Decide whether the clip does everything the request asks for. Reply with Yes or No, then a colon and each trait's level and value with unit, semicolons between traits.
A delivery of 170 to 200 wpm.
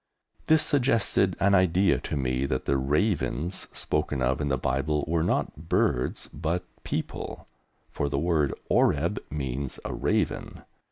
No: average, 145 wpm